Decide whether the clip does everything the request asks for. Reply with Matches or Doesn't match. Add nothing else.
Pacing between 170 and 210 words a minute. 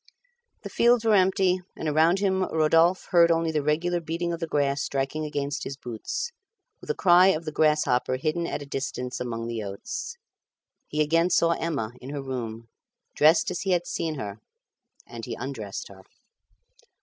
Matches